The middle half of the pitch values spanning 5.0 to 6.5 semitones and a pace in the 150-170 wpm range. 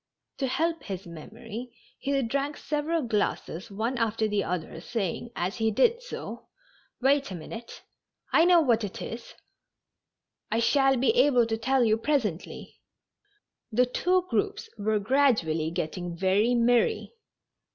No: wide, 5.4 semitones; average, 140 wpm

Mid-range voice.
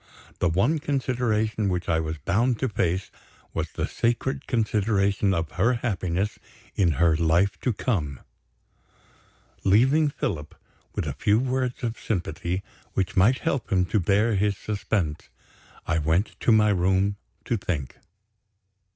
No: low, 100 Hz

